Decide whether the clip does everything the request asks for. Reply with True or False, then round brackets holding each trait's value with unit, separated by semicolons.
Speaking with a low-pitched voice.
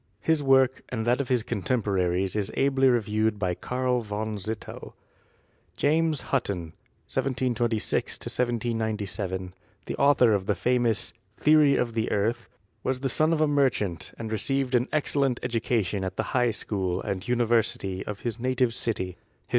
True (115 Hz)